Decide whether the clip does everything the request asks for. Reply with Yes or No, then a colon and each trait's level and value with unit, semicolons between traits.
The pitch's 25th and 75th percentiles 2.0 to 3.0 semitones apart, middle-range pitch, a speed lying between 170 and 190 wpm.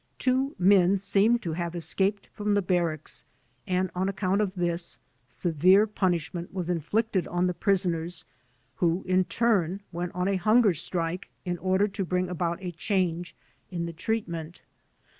No: narrow, 2.5 semitones; medium, 180 Hz; average, 160 wpm